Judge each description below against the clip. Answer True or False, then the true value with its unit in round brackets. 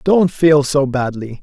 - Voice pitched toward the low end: False (145 Hz)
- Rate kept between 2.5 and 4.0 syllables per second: True (3.8 syllables/s)